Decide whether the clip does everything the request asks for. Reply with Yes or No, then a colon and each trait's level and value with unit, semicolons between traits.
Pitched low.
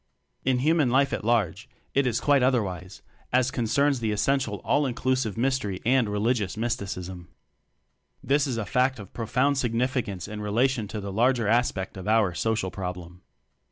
Yes: low, 115 Hz